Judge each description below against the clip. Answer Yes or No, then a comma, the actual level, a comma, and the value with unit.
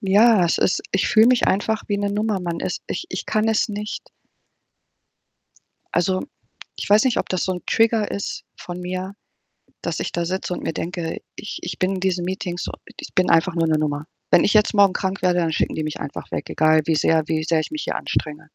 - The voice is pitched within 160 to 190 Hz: Yes, medium, 185 Hz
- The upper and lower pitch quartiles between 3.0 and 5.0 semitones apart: Yes, average, 3.7 semitones